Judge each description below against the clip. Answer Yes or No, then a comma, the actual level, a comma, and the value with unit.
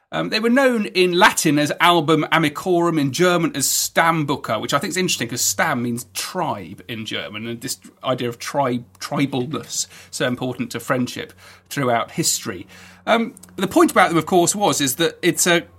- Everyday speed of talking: Yes, average, 180 wpm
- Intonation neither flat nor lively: No, wide, 5.8 semitones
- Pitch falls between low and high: Yes, medium, 150 Hz